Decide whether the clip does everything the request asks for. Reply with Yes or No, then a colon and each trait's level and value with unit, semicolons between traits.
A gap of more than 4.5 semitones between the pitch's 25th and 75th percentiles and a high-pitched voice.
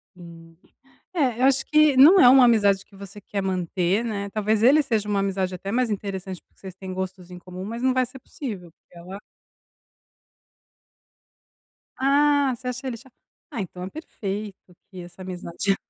Yes: average, 5.2 semitones; high, 200 Hz